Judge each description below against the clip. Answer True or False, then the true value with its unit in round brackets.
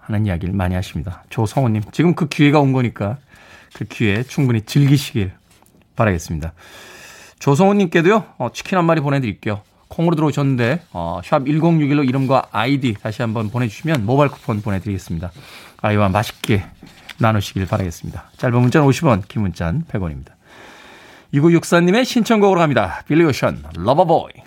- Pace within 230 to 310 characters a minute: False (365 characters per minute)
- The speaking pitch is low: True (120 Hz)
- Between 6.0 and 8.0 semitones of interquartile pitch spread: True (6.7 semitones)